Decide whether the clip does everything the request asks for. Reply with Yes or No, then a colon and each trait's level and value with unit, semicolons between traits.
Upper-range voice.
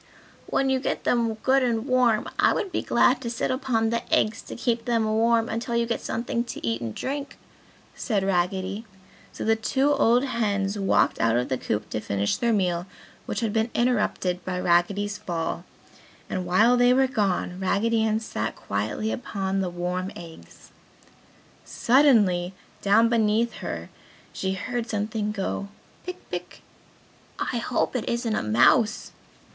Yes: high, 220 Hz